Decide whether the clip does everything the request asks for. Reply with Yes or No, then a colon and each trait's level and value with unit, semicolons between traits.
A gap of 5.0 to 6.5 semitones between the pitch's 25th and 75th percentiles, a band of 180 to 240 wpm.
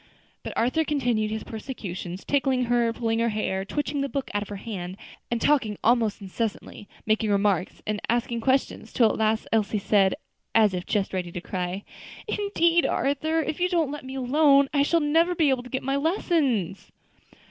Yes: average, 5.3 semitones; average, 185 wpm